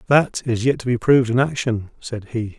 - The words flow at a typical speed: No, fast, 230 wpm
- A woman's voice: No, male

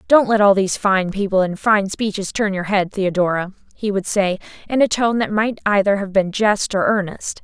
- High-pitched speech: Yes, high, 200 Hz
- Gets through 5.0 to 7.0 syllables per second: Yes, 5.1 syllables/s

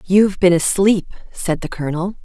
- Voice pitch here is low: No, medium, 180 Hz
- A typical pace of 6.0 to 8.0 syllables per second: No, 5.4 syllables/s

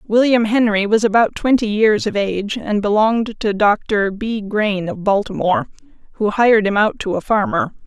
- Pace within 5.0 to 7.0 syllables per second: Yes, 5.1 syllables/s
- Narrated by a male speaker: No, female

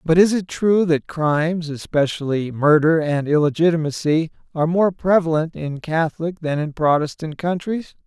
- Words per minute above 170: No, average, 140 wpm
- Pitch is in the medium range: Yes, medium, 160 Hz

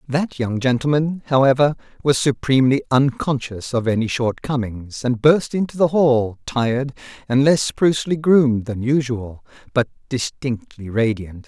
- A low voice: Yes, low, 130 Hz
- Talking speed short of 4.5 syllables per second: No, 4.6 syllables/s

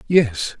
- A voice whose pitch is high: No, low, 135 Hz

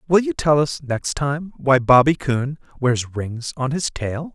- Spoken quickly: No, average, 195 wpm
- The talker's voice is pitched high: No, medium, 140 Hz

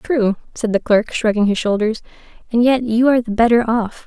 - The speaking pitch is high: Yes, high, 225 Hz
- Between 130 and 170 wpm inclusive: No, fast, 205 wpm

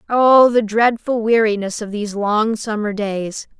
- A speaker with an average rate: Yes, average, 150 wpm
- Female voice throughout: Yes, female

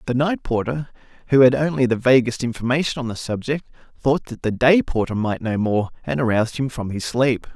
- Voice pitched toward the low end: Yes, low, 125 Hz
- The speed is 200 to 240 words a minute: Yes, fast, 205 wpm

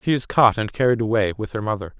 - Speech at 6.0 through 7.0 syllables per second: Yes, 6.5 syllables/s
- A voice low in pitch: Yes, low, 110 Hz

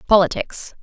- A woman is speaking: Yes, female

